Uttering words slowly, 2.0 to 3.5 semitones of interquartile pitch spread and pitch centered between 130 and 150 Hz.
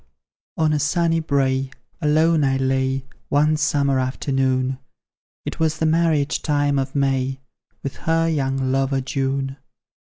Yes: slow, 130 wpm; narrow, 2.4 semitones; medium, 140 Hz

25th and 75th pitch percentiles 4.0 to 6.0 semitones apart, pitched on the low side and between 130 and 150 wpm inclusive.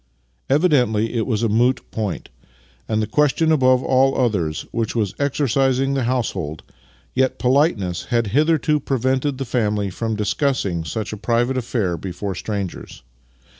Yes: average, 4.4 semitones; low, 120 Hz; average, 140 wpm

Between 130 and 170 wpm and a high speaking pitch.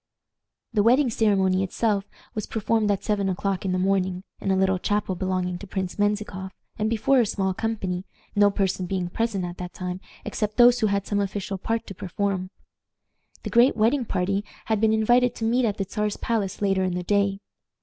No: average, 195 wpm; high, 200 Hz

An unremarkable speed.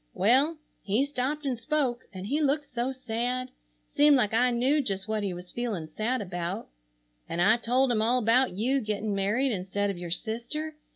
Yes: average, 185 wpm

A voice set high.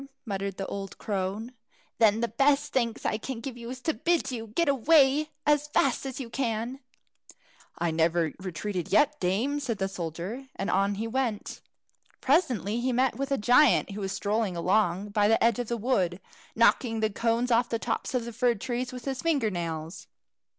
Yes: high, 230 Hz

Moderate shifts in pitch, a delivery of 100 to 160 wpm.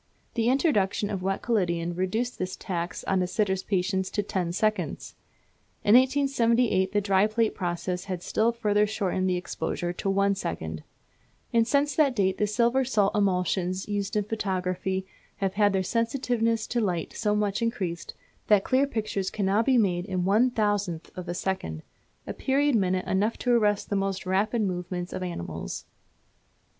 No: average, 3.5 semitones; average, 170 wpm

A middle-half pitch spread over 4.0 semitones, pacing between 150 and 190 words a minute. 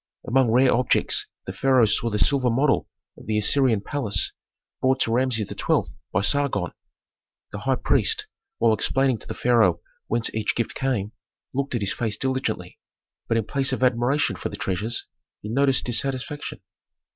No: average, 3.6 semitones; average, 165 wpm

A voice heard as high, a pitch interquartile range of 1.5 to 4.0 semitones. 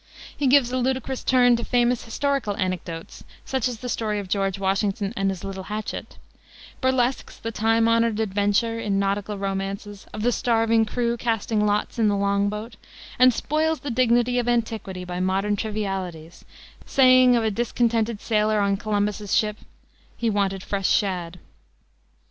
Yes: high, 215 Hz; average, 3.2 semitones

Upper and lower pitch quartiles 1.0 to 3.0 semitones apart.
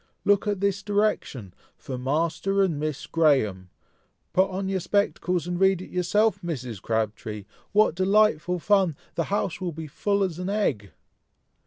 No: average, 5.2 semitones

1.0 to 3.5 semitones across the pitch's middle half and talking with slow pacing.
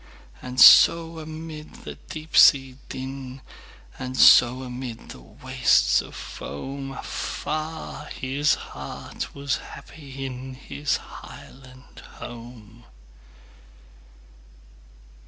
Yes: average, 2.8 semitones; slow, 80 wpm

